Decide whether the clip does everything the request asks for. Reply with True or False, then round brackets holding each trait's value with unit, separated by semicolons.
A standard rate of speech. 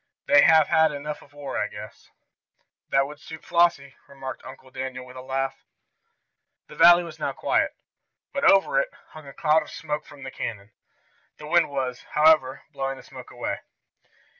True (175 wpm)